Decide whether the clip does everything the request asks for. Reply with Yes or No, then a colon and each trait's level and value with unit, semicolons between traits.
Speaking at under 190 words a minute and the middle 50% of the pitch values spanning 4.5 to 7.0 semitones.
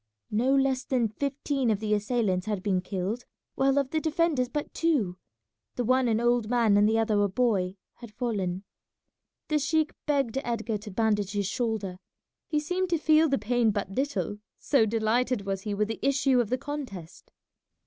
Yes: average, 180 wpm; average, 4.8 semitones